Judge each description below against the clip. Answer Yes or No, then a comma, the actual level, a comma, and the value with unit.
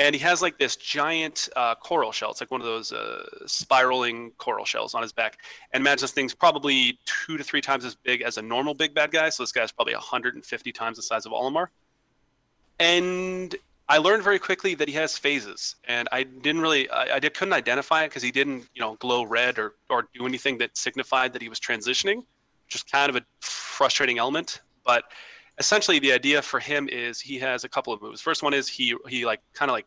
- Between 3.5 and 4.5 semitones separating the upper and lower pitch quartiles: Yes, average, 4.2 semitones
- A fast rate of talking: Yes, fast, 225 wpm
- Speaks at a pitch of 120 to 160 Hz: Yes, medium, 140 Hz